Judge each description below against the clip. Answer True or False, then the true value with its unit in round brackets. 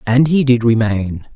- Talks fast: False (180 wpm)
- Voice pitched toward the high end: False (120 Hz)